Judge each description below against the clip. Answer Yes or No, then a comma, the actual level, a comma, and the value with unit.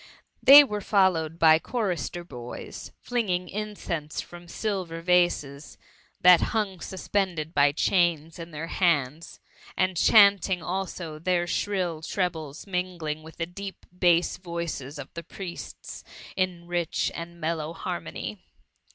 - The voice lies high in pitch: No, medium, 175 Hz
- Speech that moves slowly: Yes, slow, 130 wpm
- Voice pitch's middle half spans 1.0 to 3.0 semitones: Yes, average, 2.7 semitones